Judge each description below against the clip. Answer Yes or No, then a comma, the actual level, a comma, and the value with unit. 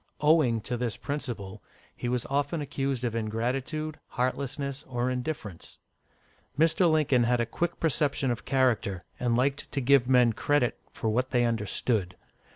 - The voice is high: No, low, 125 Hz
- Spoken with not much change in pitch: No, average, 3.3 semitones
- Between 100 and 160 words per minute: Yes, average, 150 wpm